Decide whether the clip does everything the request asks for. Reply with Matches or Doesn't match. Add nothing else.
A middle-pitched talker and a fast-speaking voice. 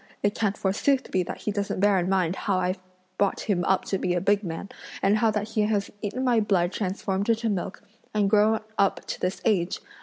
Doesn't match